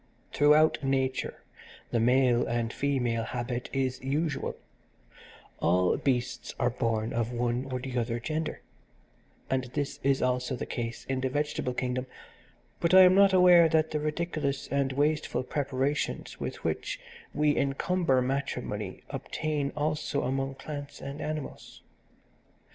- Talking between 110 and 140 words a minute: Yes, slow, 135 wpm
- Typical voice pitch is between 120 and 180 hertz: Yes, low, 135 Hz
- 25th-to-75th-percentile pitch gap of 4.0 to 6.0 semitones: No, average, 3.2 semitones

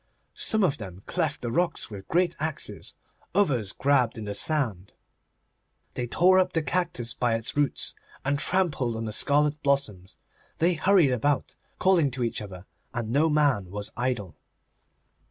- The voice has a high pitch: No, medium, 140 Hz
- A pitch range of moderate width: No, wide, 6.1 semitones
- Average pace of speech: Yes, average, 155 wpm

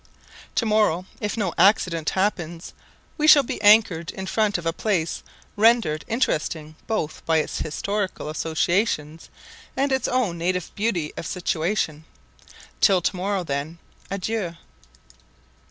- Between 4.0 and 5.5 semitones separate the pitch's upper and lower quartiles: Yes, average, 4.7 semitones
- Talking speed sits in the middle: No, slow, 130 wpm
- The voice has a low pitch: No, medium, 185 Hz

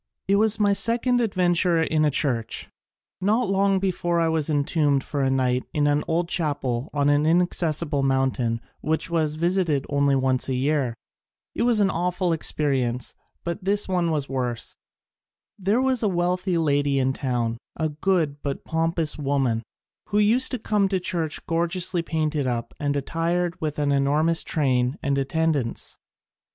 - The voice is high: No, medium, 155 Hz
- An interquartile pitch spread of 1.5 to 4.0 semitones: No, average, 4.5 semitones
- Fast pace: No, average, 165 wpm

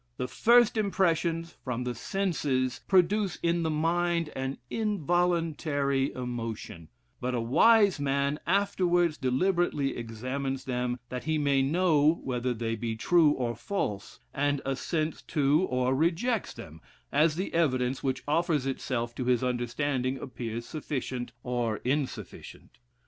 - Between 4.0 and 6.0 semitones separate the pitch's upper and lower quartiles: Yes, average, 5.1 semitones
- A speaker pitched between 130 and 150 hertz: Yes, medium, 140 Hz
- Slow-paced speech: Yes, slow, 130 wpm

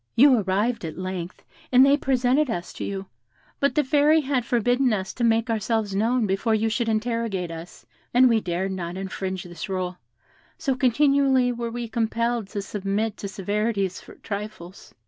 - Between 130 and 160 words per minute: No, average, 170 wpm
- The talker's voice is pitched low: No, high, 225 Hz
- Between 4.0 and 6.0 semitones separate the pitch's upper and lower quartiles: Yes, average, 4.4 semitones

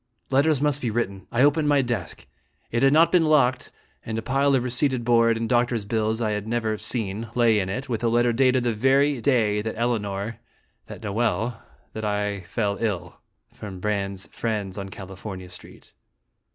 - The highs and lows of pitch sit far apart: No, average, 3.5 semitones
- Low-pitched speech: Yes, low, 115 Hz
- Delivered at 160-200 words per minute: Yes, average, 180 wpm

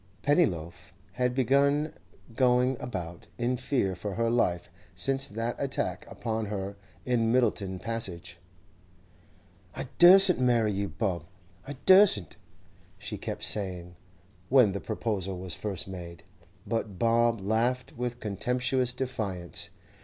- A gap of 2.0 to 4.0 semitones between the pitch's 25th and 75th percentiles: No, average, 4.8 semitones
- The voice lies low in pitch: Yes, low, 115 Hz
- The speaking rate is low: Yes, slow, 120 wpm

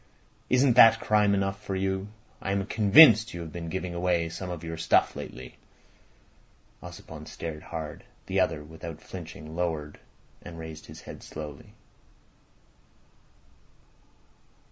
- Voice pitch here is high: No, very low, 85 Hz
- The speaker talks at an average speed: No, slow, 130 wpm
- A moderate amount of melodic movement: Yes, average, 3.3 semitones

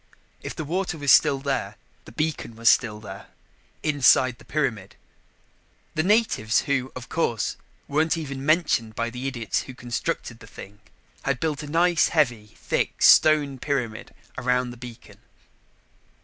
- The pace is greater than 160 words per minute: No, average, 150 wpm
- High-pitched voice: No, low, 135 Hz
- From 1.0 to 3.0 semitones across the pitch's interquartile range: No, average, 4.6 semitones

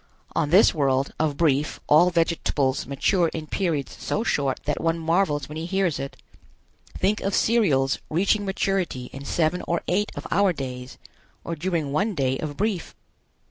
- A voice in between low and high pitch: Yes, medium, 165 Hz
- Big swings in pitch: No, average, 5.0 semitones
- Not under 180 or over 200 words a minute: No, average, 165 wpm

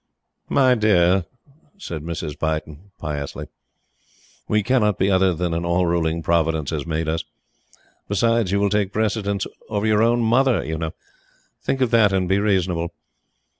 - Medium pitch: No, very low, 95 Hz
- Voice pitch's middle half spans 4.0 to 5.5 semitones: Yes, average, 4.5 semitones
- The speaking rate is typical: Yes, average, 155 wpm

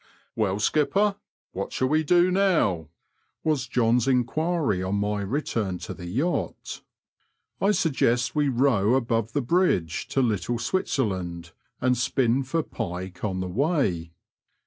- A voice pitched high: No, low, 120 Hz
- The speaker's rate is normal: Yes, average, 150 wpm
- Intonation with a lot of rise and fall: Yes, wide, 7.2 semitones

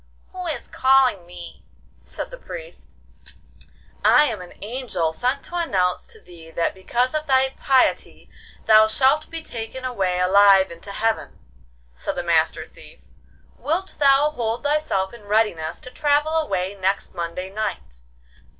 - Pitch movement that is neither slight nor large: No, wide, 7.2 semitones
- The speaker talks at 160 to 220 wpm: No, average, 145 wpm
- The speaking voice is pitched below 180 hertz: No, high, 225 Hz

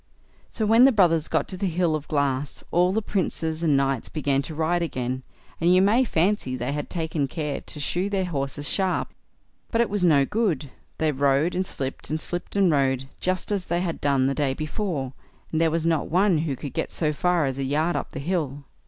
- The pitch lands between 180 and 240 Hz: No, medium, 160 Hz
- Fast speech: Yes, fast, 215 wpm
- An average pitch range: Yes, average, 4.4 semitones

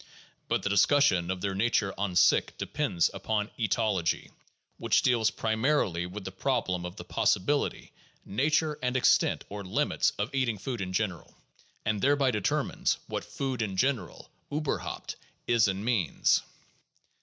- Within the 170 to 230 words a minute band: No, average, 160 wpm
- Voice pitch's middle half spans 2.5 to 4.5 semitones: No, average, 5.2 semitones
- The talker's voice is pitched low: Yes, low, 105 Hz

